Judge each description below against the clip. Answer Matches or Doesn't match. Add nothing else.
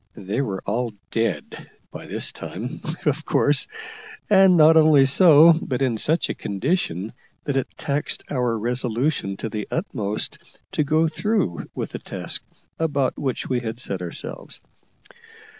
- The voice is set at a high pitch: Doesn't match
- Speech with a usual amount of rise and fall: Doesn't match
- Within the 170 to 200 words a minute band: Doesn't match